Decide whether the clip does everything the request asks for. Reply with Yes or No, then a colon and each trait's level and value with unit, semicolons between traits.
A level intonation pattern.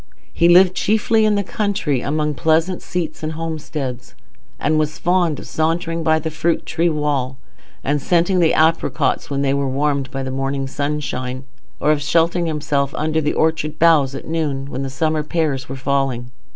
No: average, 3.2 semitones